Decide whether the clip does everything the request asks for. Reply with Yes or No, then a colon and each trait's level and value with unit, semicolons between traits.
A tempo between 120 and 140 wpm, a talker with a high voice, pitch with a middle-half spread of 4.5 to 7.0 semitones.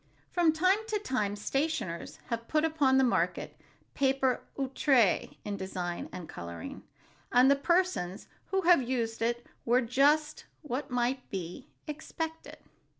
Yes: slow, 135 wpm; very high, 265 Hz; average, 5.3 semitones